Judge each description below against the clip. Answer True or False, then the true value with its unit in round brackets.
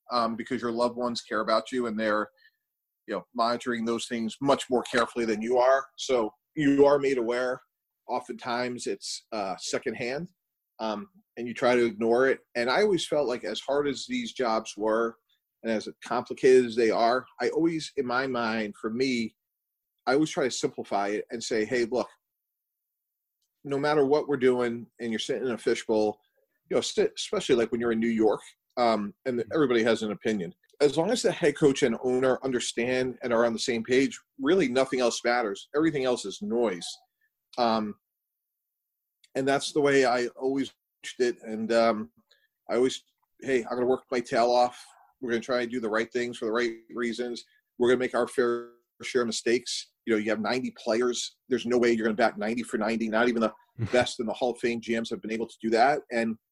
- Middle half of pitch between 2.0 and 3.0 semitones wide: True (2.6 semitones)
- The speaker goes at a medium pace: False (210 wpm)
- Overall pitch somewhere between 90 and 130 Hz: True (120 Hz)